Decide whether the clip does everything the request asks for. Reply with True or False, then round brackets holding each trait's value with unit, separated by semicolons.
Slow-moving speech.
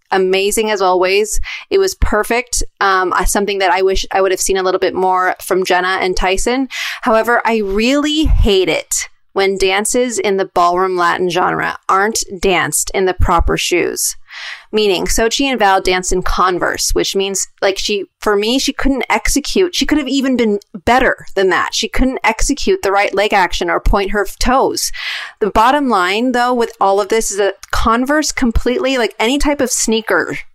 False (185 wpm)